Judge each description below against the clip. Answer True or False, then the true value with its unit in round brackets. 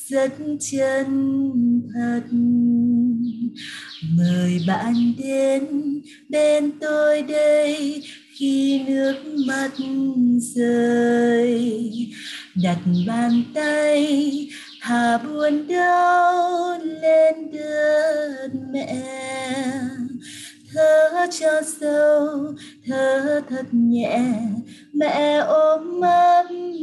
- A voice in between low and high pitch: False (275 Hz)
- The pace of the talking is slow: True (70 wpm)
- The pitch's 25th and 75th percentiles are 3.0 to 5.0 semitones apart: True (3.9 semitones)